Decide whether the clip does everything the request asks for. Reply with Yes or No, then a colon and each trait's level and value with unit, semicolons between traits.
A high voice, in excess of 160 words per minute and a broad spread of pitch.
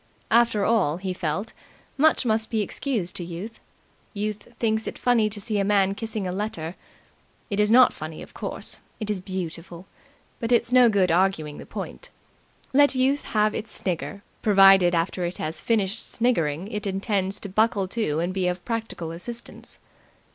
No: high, 200 Hz; average, 170 wpm; average, 3.8 semitones